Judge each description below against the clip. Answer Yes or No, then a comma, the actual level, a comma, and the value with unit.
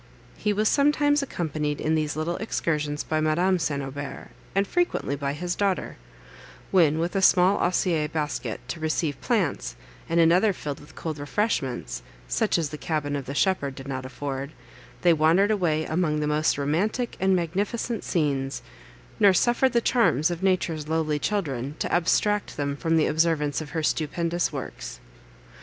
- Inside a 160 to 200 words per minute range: Yes, average, 165 wpm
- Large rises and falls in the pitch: No, average, 4.1 semitones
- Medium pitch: Yes, medium, 160 Hz